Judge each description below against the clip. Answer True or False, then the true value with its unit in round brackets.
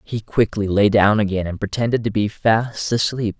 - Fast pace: False (195 wpm)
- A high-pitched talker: False (105 Hz)